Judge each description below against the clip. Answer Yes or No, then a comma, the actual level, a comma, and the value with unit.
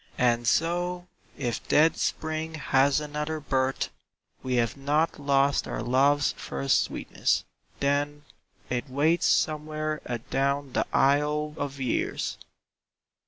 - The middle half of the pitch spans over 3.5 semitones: No, narrow, 2.5 semitones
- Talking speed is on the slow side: Yes, slow, 115 wpm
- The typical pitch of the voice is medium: Yes, medium, 145 Hz